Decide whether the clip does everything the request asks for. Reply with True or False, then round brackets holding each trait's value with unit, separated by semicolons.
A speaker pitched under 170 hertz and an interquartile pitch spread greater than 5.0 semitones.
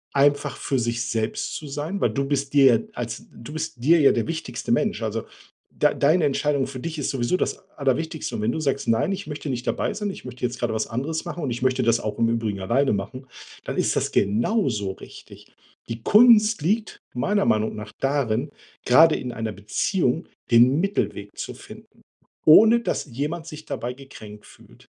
True (135 Hz; 5.4 semitones)